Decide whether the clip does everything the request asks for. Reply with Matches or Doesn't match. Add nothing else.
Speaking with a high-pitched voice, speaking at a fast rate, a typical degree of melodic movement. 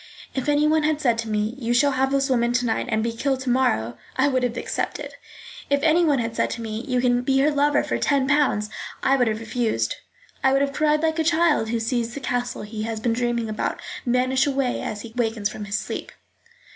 Matches